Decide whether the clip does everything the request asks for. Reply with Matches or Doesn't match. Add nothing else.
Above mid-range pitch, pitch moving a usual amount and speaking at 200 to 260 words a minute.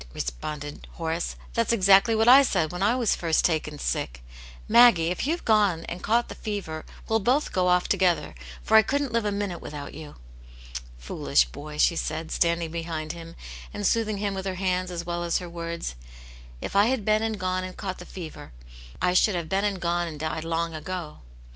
Doesn't match